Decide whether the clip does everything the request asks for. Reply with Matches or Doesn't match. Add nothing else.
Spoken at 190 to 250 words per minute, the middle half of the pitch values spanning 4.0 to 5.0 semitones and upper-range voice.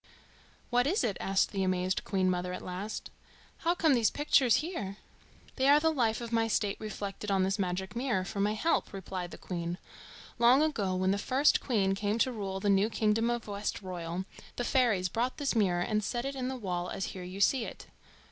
Matches